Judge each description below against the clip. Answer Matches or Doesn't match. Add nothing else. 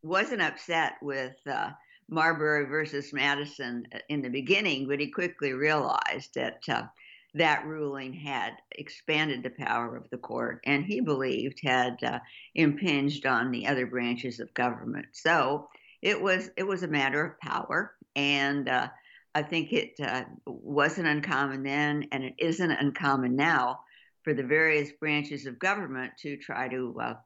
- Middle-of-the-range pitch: Matches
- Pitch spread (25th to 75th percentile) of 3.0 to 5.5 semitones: Doesn't match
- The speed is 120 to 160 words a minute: Matches